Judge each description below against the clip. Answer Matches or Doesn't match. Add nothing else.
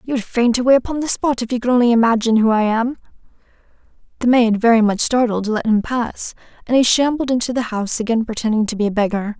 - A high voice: Matches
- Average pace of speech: Doesn't match